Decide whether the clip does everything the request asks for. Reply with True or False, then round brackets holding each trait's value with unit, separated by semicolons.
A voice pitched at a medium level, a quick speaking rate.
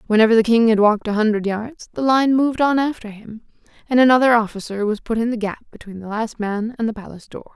False (225 Hz; 240 wpm)